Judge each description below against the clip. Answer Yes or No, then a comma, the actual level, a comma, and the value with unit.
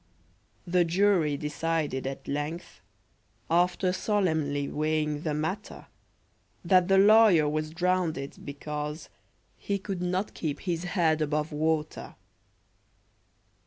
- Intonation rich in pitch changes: No, average, 3.3 semitones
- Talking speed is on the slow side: Yes, slow, 105 wpm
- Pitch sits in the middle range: Yes, medium, 160 Hz